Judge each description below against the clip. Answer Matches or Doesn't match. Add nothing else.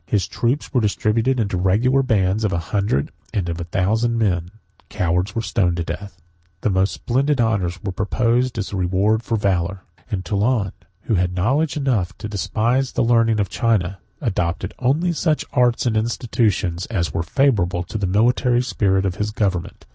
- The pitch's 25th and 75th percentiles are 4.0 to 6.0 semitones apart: Matches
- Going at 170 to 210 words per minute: Matches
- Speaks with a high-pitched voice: Doesn't match